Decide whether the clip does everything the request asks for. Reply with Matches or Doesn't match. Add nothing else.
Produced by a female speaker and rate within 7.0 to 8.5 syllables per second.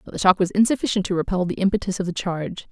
Matches